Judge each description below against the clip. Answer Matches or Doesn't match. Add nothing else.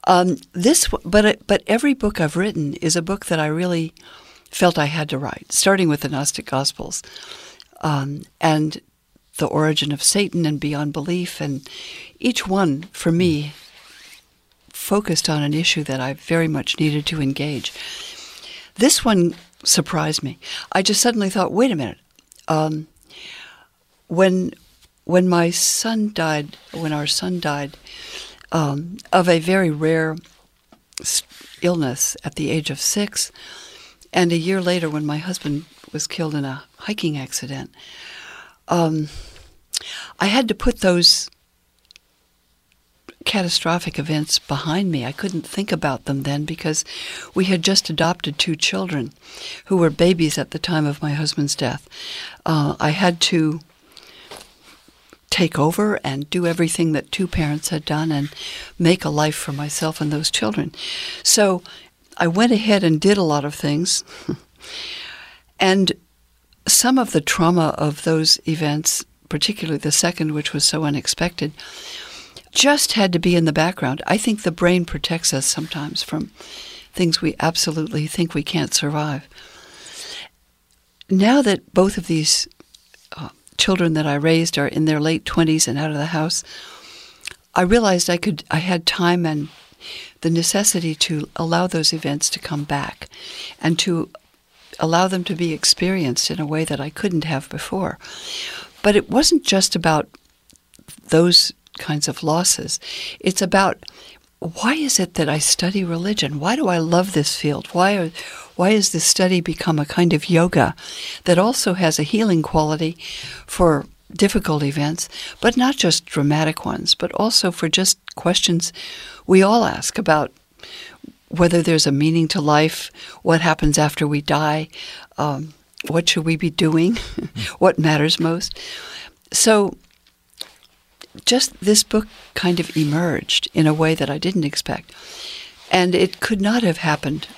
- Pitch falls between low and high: Matches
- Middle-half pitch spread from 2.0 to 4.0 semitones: Matches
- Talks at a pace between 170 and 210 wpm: Doesn't match